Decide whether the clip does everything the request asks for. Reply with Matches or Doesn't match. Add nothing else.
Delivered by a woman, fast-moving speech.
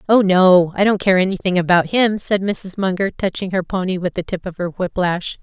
Matches